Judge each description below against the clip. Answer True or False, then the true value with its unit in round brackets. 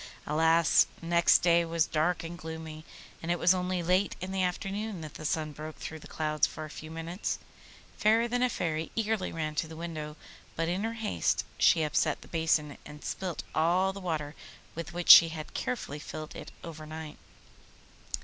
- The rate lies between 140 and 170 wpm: False (185 wpm)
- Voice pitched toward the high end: False (165 Hz)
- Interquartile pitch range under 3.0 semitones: True (2.6 semitones)